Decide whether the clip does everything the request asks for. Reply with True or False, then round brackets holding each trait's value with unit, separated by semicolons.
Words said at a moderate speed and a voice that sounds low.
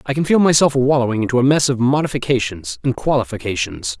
True (180 wpm; 125 Hz)